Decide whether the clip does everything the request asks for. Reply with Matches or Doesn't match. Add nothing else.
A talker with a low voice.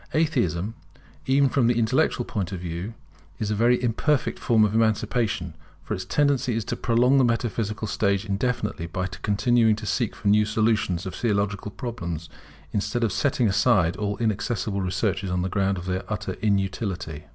Matches